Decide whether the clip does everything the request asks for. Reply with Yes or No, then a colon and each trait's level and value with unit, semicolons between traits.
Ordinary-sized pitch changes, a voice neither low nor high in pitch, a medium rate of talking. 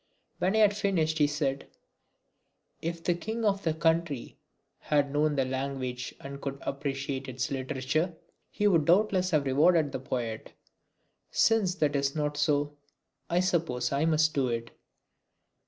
Yes: average, 3.7 semitones; medium, 150 Hz; average, 150 wpm